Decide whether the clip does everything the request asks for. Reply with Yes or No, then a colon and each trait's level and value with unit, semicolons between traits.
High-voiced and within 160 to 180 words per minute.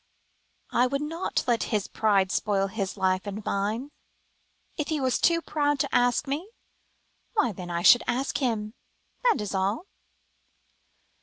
No: high, 235 Hz; average, 150 wpm